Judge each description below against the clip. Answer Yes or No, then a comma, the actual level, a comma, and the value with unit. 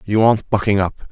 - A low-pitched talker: Yes, low, 105 Hz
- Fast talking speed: Yes, fast, 215 wpm